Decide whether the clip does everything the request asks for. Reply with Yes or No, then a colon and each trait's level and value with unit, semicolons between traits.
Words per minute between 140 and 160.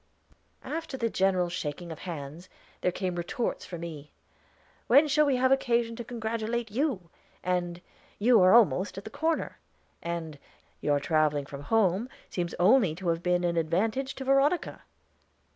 Yes: average, 155 wpm